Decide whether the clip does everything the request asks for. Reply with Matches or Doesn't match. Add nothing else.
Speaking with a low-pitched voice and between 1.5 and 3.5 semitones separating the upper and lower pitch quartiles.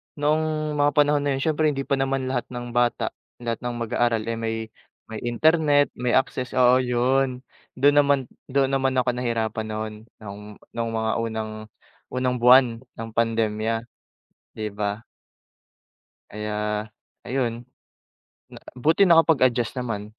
Matches